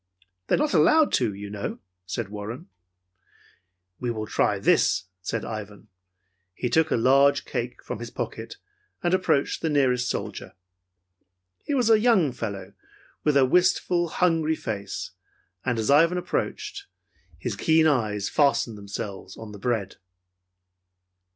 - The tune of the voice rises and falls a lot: Yes, wide, 7.6 semitones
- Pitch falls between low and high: No, low, 125 Hz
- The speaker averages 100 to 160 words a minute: Yes, average, 140 wpm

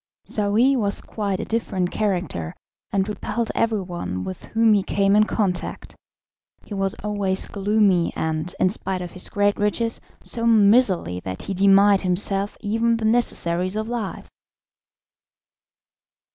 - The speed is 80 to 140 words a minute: Yes, slow, 135 wpm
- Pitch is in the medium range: No, high, 200 Hz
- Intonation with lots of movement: No, average, 2.9 semitones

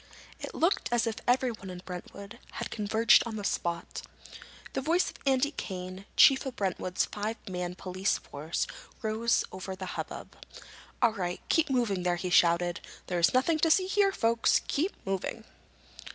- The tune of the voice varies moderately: No, wide, 5.7 semitones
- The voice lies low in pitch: No, high, 210 Hz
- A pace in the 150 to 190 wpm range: Yes, average, 160 wpm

